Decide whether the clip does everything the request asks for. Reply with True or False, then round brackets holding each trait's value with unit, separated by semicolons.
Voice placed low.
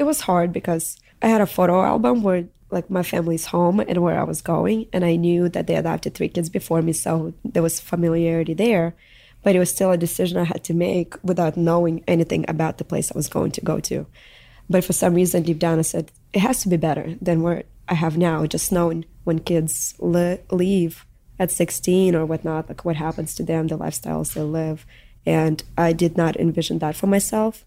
False (170 Hz)